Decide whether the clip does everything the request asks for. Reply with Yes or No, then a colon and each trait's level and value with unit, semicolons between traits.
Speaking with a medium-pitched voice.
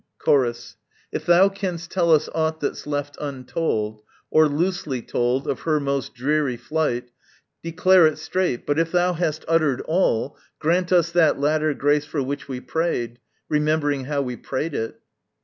Yes: medium, 150 Hz